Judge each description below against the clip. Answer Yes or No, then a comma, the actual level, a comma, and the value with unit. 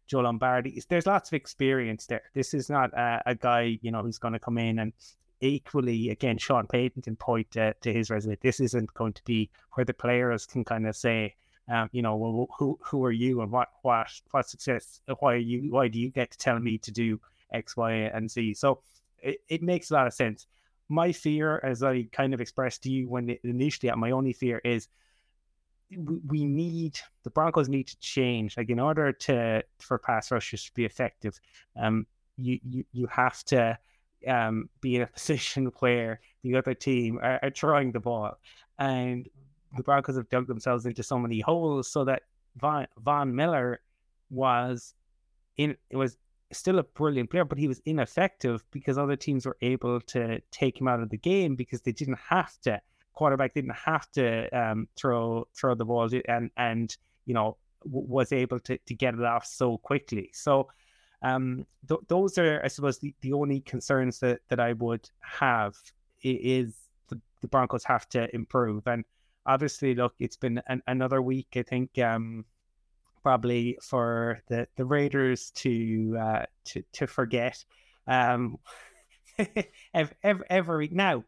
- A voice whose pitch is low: Yes, low, 125 Hz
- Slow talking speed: No, average, 180 wpm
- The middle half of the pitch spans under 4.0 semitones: Yes, average, 2.8 semitones